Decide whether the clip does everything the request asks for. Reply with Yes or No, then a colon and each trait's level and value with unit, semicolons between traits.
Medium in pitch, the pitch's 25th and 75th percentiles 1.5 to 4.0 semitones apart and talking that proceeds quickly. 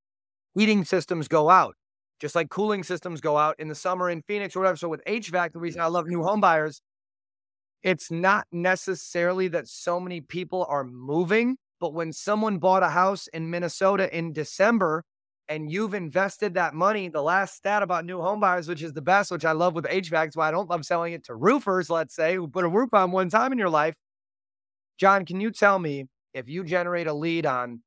Yes: medium, 175 Hz; average, 3.3 semitones; fast, 210 wpm